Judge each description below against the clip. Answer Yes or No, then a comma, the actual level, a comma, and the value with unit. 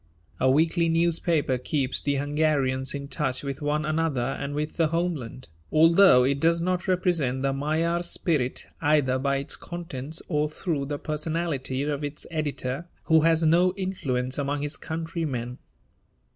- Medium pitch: Yes, medium, 150 Hz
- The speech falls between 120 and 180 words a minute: Yes, average, 150 wpm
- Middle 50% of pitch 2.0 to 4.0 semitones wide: Yes, average, 3.3 semitones